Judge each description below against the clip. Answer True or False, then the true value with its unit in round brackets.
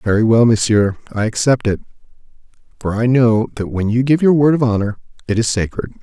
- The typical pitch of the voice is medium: False (115 Hz)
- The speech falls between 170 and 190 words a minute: False (200 wpm)